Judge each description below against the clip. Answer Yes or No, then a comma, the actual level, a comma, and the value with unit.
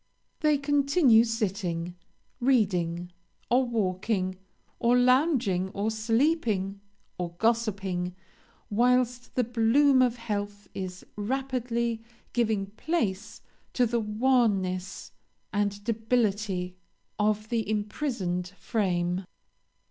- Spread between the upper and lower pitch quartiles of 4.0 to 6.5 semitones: Yes, average, 4.3 semitones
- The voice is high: Yes, high, 220 Hz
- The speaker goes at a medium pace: No, slow, 90 wpm